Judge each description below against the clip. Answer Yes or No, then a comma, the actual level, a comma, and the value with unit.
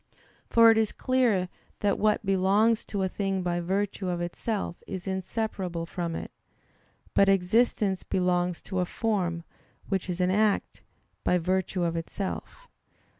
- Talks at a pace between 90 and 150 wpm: Yes, average, 145 wpm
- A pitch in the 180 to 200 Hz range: Yes, high, 190 Hz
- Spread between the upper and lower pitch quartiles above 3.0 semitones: No, average, 2.7 semitones